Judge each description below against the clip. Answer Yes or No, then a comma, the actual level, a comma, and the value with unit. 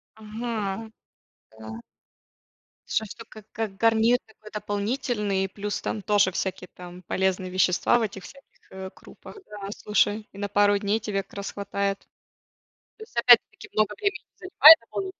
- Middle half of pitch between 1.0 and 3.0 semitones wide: Yes, narrow, 2.5 semitones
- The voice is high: Yes, high, 205 Hz